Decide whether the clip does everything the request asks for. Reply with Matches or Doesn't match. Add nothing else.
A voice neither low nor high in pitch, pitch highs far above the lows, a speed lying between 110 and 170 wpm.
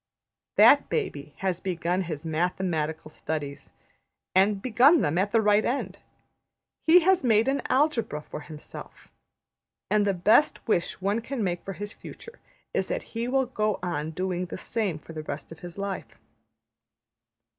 Doesn't match